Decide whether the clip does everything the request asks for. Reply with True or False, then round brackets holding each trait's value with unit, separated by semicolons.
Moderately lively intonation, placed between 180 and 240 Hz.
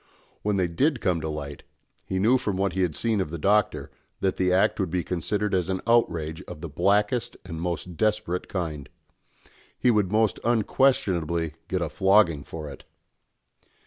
False (4.1 semitones; 95 Hz)